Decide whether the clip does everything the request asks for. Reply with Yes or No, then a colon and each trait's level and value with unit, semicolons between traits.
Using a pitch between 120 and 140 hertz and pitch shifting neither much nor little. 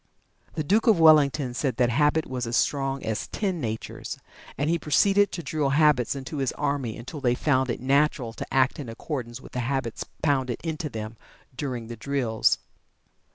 Yes: low, 135 Hz; average, 3.8 semitones